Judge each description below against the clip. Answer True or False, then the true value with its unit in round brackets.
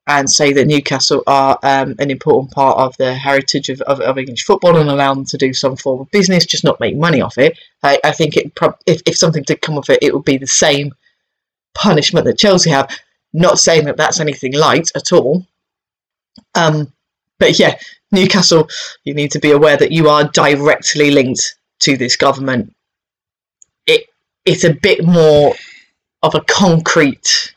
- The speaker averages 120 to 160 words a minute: False (185 wpm)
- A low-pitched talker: False (145 Hz)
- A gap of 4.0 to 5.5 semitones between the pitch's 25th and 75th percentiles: True (4.3 semitones)